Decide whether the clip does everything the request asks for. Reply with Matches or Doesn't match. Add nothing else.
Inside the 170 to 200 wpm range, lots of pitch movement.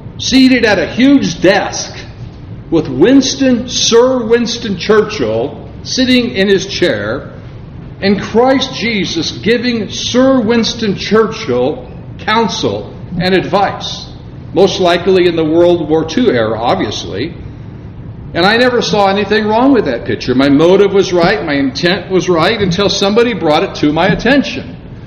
Doesn't match